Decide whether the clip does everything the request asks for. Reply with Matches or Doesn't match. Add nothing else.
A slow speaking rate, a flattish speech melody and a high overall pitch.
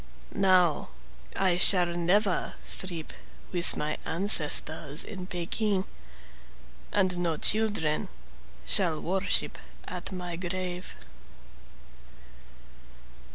Doesn't match